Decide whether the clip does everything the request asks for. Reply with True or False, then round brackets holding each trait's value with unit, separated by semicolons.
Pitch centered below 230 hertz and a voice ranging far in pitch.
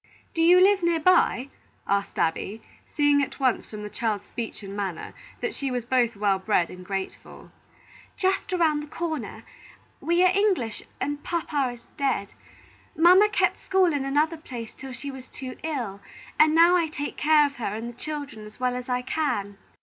False (275 Hz; 6.3 semitones)